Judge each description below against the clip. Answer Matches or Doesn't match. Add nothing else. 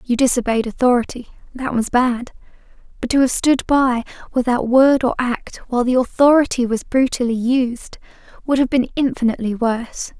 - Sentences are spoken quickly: Doesn't match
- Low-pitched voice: Doesn't match